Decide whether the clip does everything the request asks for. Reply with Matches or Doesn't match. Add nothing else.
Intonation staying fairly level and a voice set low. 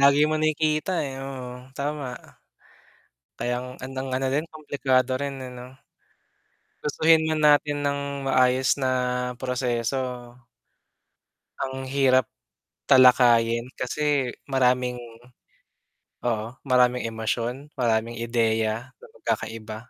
Matches